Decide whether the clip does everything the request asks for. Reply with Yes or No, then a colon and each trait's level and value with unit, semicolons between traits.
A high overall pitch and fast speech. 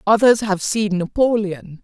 No: high, 205 Hz; slow, 130 wpm